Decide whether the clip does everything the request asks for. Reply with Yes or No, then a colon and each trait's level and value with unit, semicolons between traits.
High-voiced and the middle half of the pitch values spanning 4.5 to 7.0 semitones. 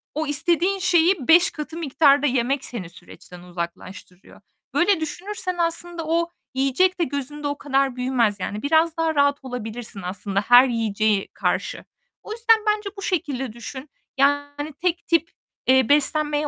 Yes: very high, 285 Hz; wide, 5.4 semitones